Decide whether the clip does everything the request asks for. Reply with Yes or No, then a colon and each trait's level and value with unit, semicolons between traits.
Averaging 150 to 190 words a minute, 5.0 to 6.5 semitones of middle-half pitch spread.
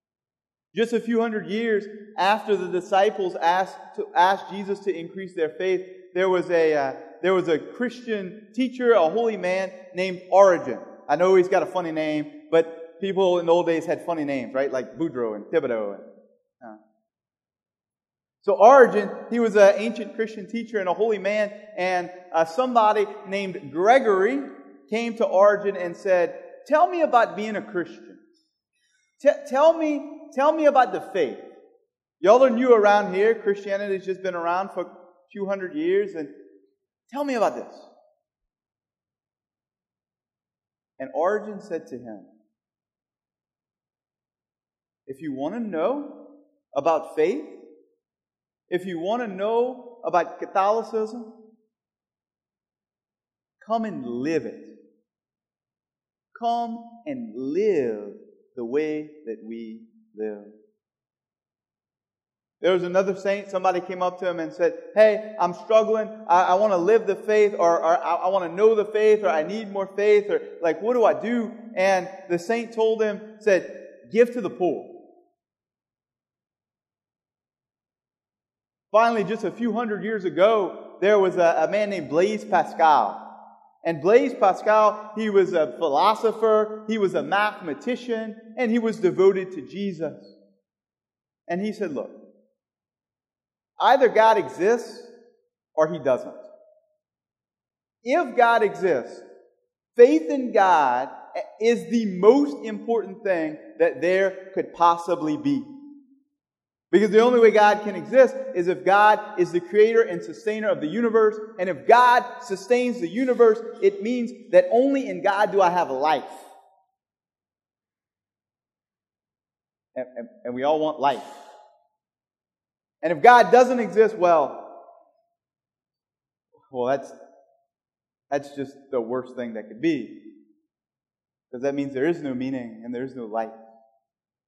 No: average, 140 wpm; wide, 5.6 semitones